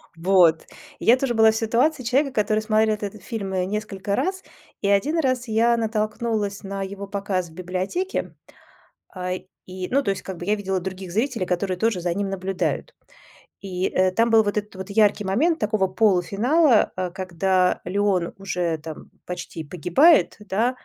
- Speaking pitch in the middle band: No, high, 200 Hz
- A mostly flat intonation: No, average, 3.3 semitones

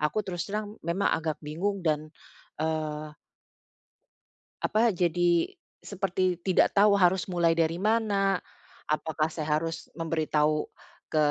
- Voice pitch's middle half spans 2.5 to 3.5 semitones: No, average, 3.9 semitones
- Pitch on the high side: No, medium, 170 Hz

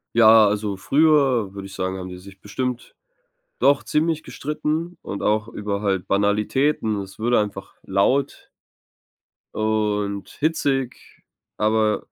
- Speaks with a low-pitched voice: Yes, low, 110 Hz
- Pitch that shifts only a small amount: No, average, 5.0 semitones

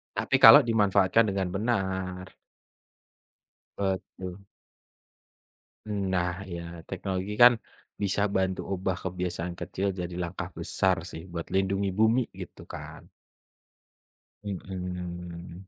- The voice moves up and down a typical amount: No, narrow, 1.7 semitones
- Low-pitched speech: Yes, very low, 95 Hz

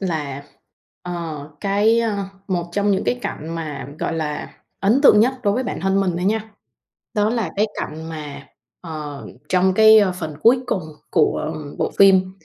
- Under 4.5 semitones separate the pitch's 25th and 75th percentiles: No, average, 5.0 semitones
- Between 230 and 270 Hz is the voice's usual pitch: No, medium, 185 Hz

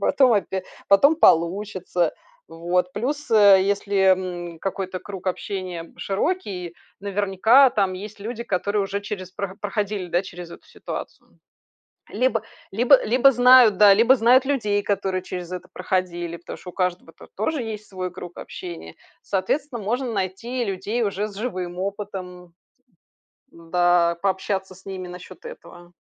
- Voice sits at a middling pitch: No, high, 195 Hz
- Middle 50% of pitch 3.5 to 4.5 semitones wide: No, average, 2.8 semitones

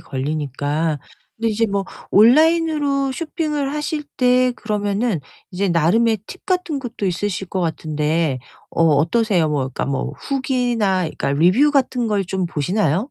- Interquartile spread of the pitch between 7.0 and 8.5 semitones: Yes, wide, 7.9 semitones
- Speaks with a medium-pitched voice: No, high, 205 Hz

